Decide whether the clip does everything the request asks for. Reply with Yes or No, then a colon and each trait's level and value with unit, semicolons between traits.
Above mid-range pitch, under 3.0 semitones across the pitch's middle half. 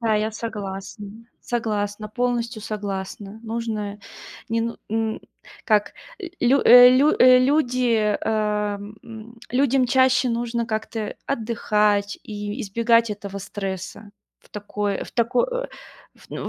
Yes: high, 220 Hz; narrow, 2.6 semitones